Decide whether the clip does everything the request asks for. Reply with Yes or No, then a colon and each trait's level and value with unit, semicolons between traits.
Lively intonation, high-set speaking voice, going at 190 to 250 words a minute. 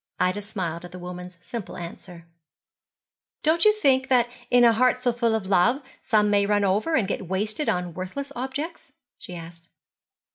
No: wide, 5.8 semitones; high, 205 Hz; average, 175 wpm